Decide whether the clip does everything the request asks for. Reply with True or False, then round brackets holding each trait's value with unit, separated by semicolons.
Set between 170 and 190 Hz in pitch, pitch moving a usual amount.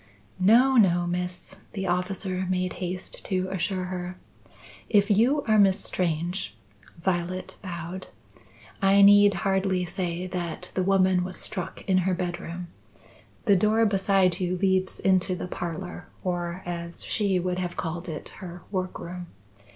False (185 Hz; 1.5 semitones)